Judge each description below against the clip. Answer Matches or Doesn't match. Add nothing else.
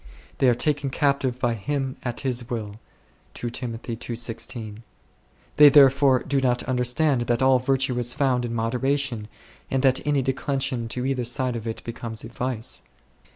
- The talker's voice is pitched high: Doesn't match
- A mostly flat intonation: Matches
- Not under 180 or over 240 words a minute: Doesn't match